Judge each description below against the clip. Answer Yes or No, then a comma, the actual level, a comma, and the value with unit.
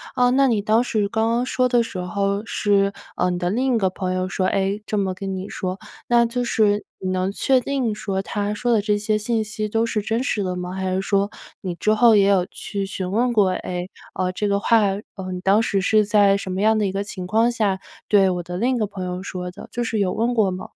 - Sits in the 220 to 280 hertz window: No, high, 205 Hz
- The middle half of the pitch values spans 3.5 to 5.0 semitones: No, average, 2.9 semitones